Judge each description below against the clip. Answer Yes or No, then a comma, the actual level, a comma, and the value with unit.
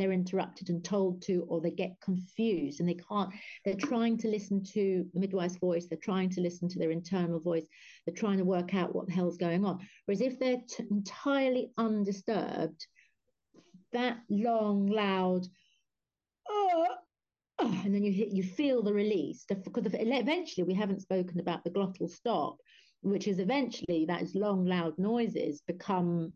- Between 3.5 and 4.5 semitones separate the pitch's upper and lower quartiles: Yes, average, 3.8 semitones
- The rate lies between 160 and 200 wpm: Yes, average, 170 wpm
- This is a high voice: Yes, high, 195 Hz